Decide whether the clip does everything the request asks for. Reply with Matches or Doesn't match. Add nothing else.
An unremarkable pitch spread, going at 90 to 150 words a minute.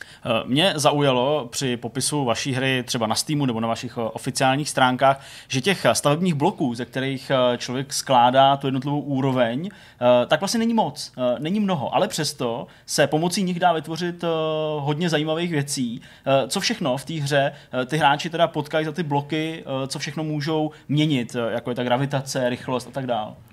Doesn't match